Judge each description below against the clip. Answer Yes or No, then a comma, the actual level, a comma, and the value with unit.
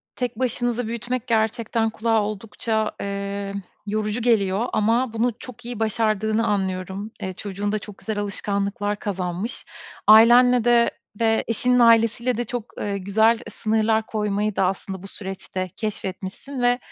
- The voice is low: No, high, 220 Hz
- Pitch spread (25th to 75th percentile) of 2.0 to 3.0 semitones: Yes, narrow, 2.6 semitones